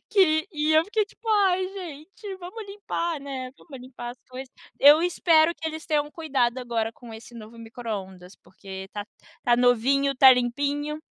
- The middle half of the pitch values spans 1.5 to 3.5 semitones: No, wide, 5.6 semitones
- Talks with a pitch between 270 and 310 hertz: Yes, very high, 280 Hz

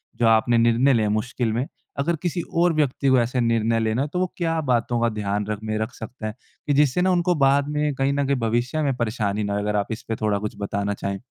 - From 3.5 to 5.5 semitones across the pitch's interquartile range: Yes, average, 4.6 semitones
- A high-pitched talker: No, low, 120 Hz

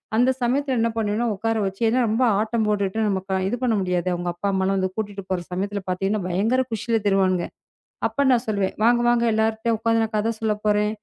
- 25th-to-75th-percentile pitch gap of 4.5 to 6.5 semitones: No, average, 2.9 semitones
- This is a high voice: Yes, high, 210 Hz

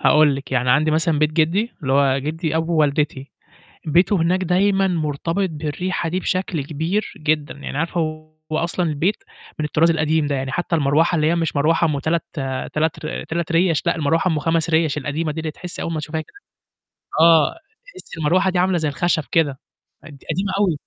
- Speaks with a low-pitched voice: No, medium, 160 Hz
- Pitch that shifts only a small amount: Yes, narrow, 2.3 semitones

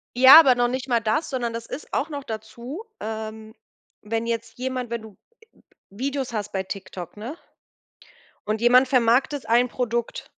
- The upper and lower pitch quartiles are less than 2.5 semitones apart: No, average, 2.9 semitones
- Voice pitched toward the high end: Yes, high, 240 Hz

